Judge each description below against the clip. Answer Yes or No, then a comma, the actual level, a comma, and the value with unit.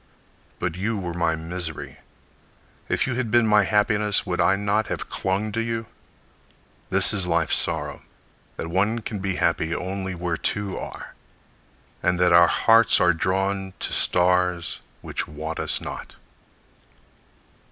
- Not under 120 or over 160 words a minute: Yes, average, 145 wpm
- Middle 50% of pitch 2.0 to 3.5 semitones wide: Yes, average, 3.1 semitones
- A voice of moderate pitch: No, very low, 95 Hz